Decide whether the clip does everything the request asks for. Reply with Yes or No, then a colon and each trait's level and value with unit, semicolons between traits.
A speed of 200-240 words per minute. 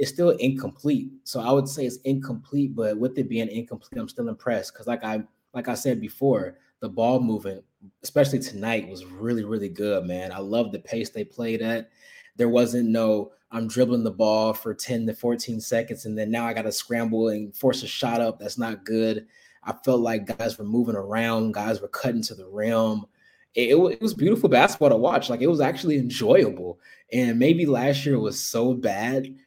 Yes: fast, 205 wpm